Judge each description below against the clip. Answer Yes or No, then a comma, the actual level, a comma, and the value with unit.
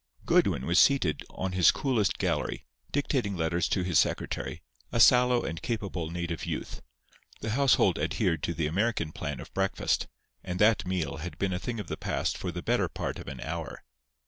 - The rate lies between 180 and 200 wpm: Yes, average, 185 wpm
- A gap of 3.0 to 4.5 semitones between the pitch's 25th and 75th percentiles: No, average, 5.1 semitones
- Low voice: Yes, very low, 90 Hz